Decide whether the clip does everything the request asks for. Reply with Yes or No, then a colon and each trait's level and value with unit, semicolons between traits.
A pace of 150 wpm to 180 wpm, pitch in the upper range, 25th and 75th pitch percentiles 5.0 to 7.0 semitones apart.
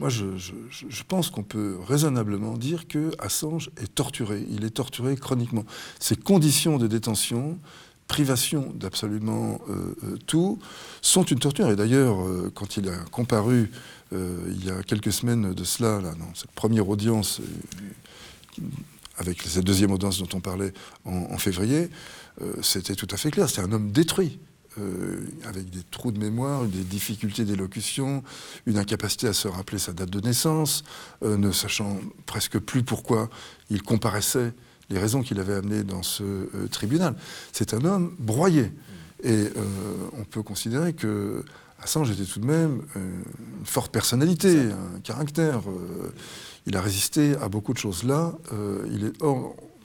No: average, 160 wpm; low, 110 Hz; wide, 5.4 semitones